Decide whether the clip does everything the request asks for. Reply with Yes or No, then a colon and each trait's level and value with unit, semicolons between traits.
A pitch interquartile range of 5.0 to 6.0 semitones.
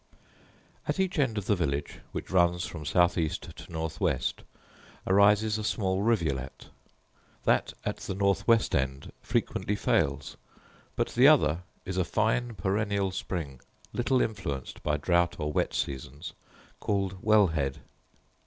Yes: wide, 5.5 semitones